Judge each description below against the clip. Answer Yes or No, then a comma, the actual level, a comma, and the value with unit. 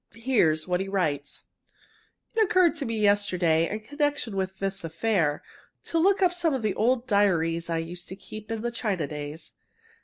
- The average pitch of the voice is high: Yes, high, 200 Hz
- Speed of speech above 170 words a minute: Yes, average, 180 wpm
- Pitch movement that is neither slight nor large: No, wide, 6.2 semitones